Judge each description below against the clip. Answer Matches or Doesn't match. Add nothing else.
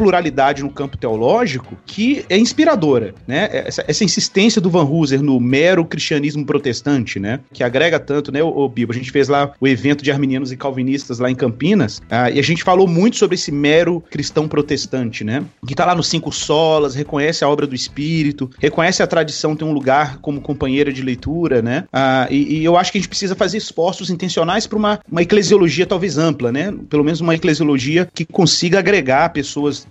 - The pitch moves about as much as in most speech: Matches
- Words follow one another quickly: Matches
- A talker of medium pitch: Matches